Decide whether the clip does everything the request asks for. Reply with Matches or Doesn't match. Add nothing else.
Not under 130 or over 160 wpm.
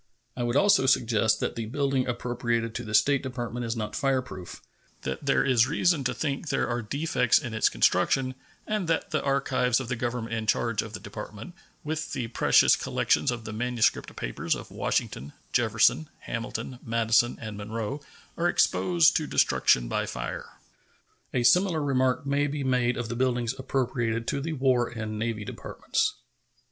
Doesn't match